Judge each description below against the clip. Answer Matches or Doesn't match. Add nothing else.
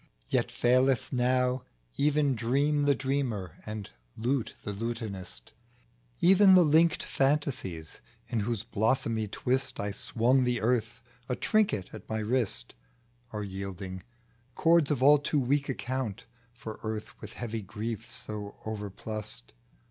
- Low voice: Matches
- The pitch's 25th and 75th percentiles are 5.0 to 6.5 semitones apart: Doesn't match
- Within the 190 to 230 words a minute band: Doesn't match